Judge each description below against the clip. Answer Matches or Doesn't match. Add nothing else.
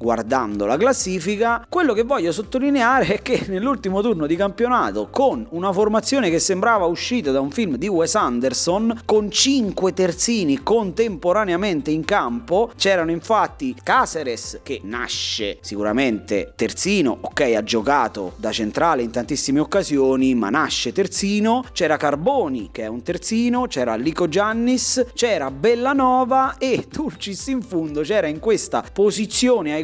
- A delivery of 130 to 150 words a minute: Matches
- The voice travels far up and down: Matches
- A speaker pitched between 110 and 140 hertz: Doesn't match